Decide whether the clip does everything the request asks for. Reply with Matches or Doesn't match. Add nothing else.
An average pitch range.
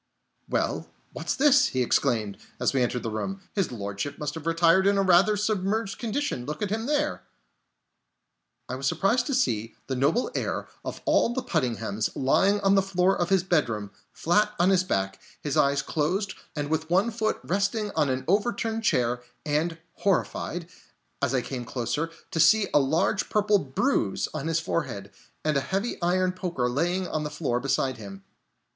Doesn't match